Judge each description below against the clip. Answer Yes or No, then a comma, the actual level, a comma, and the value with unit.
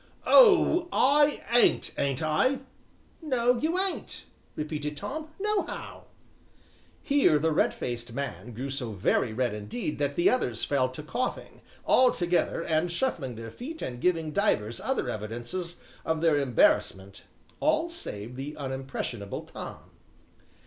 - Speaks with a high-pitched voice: No, medium, 150 Hz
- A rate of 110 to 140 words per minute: Yes, slow, 135 wpm